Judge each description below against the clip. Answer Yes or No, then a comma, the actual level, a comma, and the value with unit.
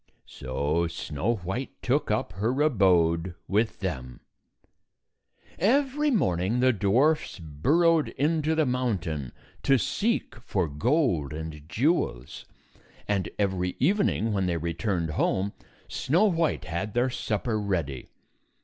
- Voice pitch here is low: Yes, low, 105 Hz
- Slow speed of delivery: Yes, slow, 115 wpm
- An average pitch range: No, wide, 8.6 semitones